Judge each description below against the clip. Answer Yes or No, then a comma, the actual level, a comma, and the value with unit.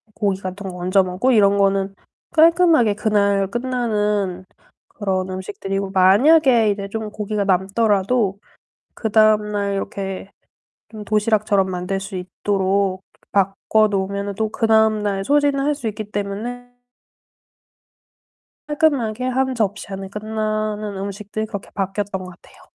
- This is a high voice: Yes, high, 205 Hz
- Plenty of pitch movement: No, narrow, 2.1 semitones